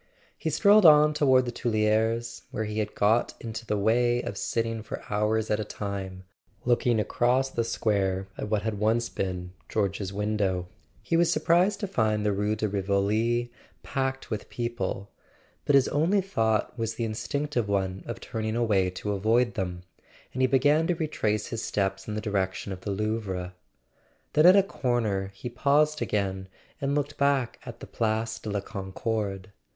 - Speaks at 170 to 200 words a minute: Yes, average, 175 wpm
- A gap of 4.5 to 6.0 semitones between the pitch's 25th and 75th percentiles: No, average, 3.6 semitones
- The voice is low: Yes, low, 110 Hz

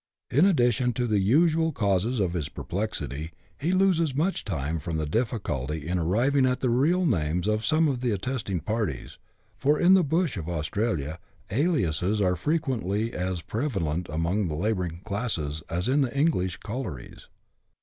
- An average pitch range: No, wide, 7.9 semitones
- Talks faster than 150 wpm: Yes, average, 165 wpm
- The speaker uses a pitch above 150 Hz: No, low, 105 Hz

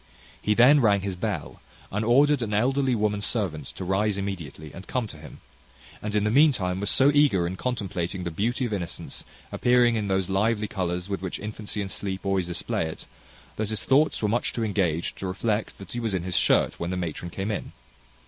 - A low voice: Yes, low, 100 Hz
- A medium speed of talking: No, fast, 210 wpm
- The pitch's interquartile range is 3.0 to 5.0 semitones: Yes, average, 3.7 semitones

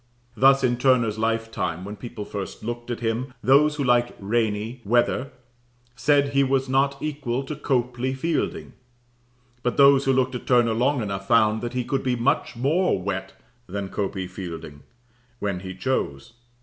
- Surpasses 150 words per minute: Yes, average, 160 wpm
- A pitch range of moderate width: Yes, average, 4.4 semitones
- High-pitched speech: No, low, 120 Hz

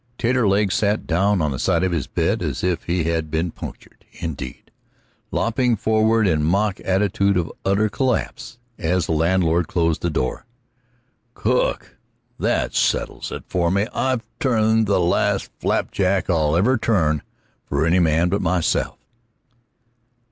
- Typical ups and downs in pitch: Yes, average, 4.5 semitones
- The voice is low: Yes, very low, 95 Hz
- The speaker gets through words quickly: No, average, 145 wpm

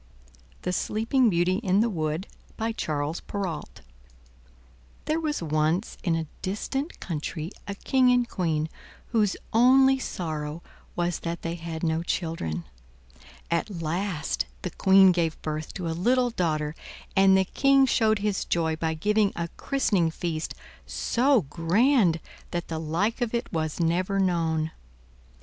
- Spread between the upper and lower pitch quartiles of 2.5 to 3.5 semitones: No, average, 5.2 semitones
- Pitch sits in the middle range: Yes, medium, 175 Hz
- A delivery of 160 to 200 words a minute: No, average, 140 wpm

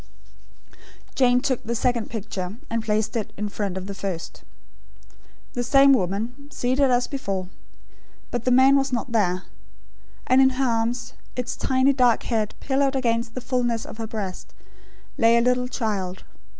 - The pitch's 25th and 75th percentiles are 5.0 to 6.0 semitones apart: No, average, 3.1 semitones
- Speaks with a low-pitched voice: No, high, 235 Hz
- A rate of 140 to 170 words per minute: Yes, average, 160 wpm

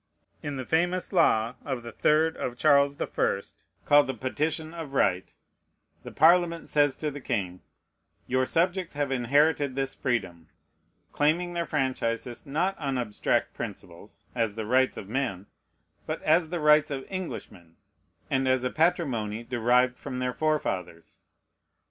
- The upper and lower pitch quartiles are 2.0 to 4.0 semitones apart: No, average, 4.5 semitones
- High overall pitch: No, low, 135 Hz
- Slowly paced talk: No, average, 150 wpm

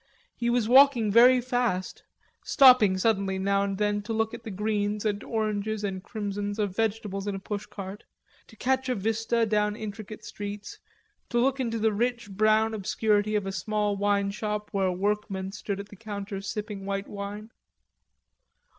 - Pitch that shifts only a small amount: Yes, narrow, 1.9 semitones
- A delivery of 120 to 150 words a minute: No, average, 170 wpm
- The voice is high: Yes, high, 210 Hz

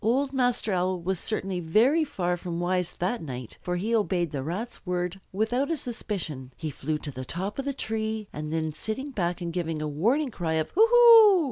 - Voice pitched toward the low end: No, medium, 185 Hz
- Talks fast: Yes, fast, 210 wpm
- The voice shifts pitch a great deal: Yes, wide, 6.6 semitones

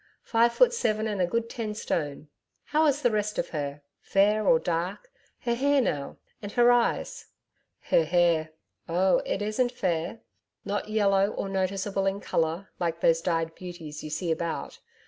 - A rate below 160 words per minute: No, average, 165 wpm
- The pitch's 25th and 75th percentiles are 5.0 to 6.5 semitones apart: Yes, average, 5.3 semitones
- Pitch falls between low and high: No, high, 195 Hz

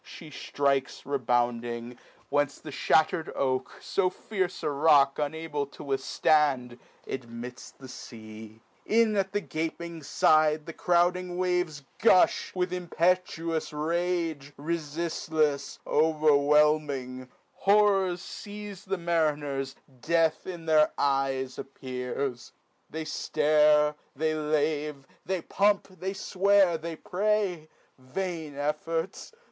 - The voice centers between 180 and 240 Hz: No, medium, 155 Hz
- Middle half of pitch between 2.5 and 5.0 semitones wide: Yes, average, 4.1 semitones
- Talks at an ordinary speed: No, slow, 105 wpm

